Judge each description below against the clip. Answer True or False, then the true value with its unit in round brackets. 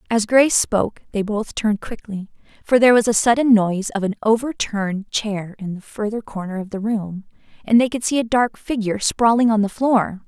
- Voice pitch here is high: True (215 Hz)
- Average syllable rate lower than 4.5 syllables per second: False (5.5 syllables/s)